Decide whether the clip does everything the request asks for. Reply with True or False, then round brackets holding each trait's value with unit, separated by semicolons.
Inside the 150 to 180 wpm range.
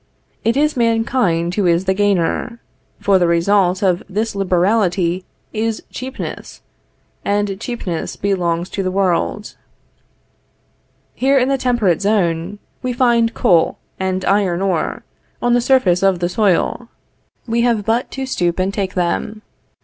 False (140 wpm)